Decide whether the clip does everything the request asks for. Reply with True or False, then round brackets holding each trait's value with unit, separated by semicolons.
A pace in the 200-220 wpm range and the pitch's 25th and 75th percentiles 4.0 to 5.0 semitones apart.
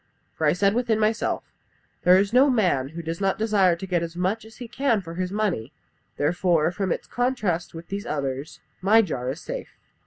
True (205 wpm; 4.7 semitones)